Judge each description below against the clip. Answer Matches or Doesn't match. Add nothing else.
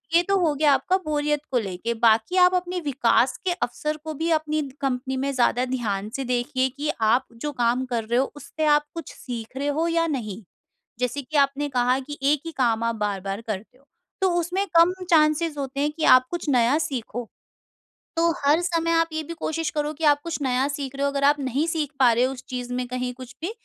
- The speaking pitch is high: Matches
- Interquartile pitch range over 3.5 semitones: Matches